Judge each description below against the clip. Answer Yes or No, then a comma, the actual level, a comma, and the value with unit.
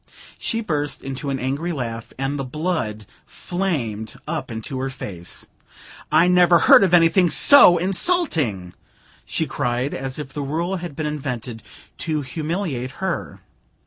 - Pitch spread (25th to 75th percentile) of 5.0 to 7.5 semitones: Yes, average, 5.3 semitones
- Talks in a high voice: No, medium, 145 Hz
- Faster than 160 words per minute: No, average, 145 wpm